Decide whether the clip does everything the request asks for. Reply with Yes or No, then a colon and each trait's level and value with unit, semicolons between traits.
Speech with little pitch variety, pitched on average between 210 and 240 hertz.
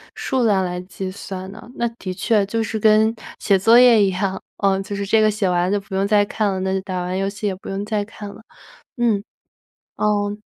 No: narrow, 2.0 semitones; high, 200 Hz